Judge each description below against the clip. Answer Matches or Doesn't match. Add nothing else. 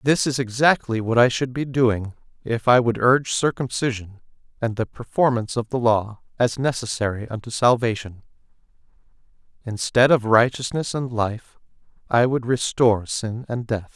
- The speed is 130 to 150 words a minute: Matches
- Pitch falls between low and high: Doesn't match